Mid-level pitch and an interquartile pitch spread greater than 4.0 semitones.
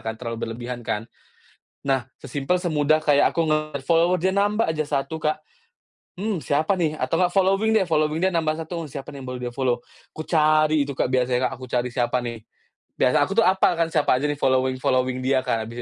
Yes: medium, 150 Hz; average, 4.5 semitones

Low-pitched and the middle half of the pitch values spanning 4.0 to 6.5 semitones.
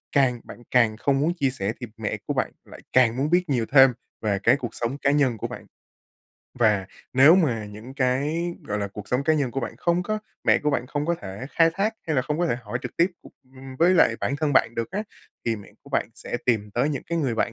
Yes: low, 130 Hz; average, 4.6 semitones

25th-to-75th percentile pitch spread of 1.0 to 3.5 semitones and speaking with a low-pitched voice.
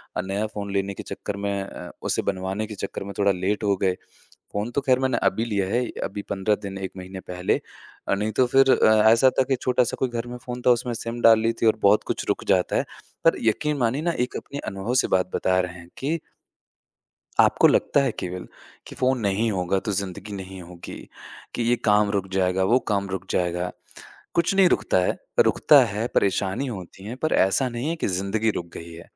No: average, 4.1 semitones; low, 105 Hz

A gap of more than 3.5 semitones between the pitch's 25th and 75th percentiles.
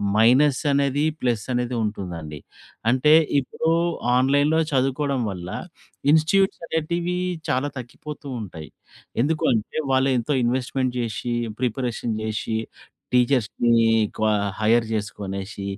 Yes: average, 4.7 semitones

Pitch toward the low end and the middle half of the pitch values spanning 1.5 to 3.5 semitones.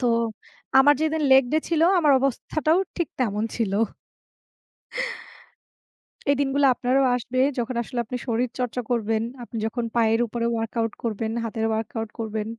No: high, 240 Hz; average, 3.2 semitones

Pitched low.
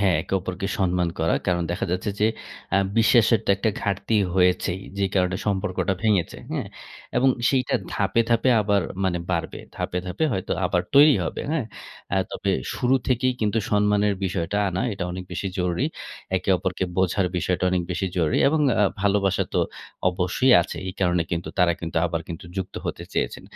Yes: very low, 95 Hz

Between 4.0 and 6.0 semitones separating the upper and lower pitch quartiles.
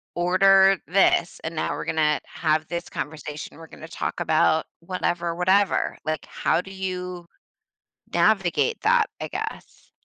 No: average, 3.2 semitones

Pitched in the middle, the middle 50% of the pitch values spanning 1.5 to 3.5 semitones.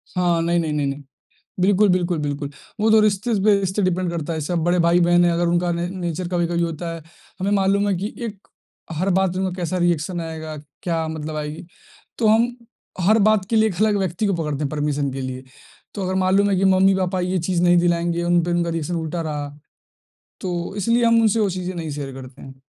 Yes: medium, 175 Hz; average, 2.9 semitones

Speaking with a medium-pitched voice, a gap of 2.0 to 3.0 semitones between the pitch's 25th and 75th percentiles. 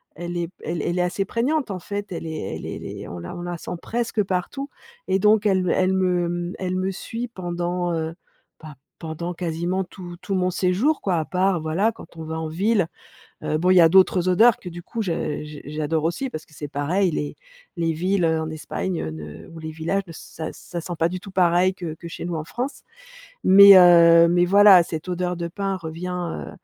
Yes: medium, 175 Hz; narrow, 2.6 semitones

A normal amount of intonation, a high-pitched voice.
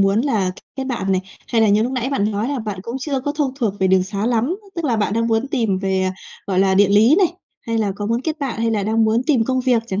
Yes: average, 4.4 semitones; high, 225 Hz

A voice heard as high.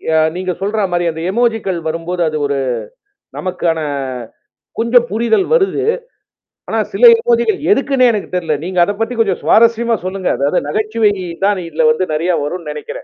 Yes: high, 200 Hz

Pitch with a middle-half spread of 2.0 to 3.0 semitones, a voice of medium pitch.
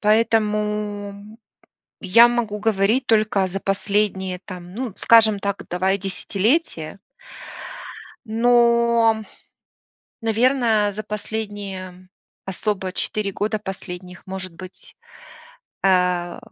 No: average, 2.7 semitones; high, 205 Hz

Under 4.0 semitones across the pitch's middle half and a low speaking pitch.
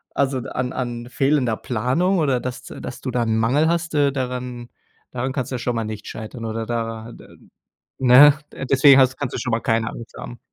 Yes: narrow, 2.5 semitones; low, 125 Hz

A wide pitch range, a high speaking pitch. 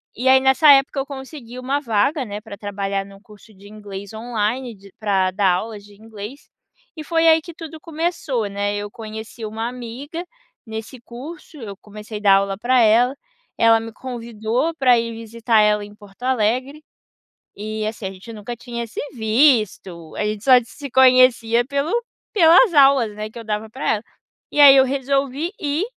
No: average, 4.2 semitones; high, 230 Hz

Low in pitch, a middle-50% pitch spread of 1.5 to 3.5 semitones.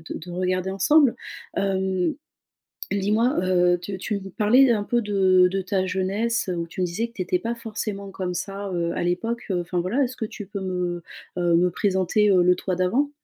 No: high, 190 Hz; average, 2.8 semitones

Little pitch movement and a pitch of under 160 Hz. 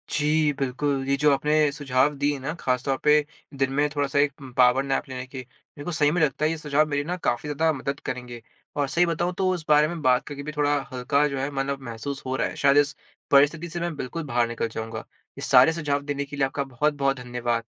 Yes: narrow, 2.2 semitones; medium, 140 Hz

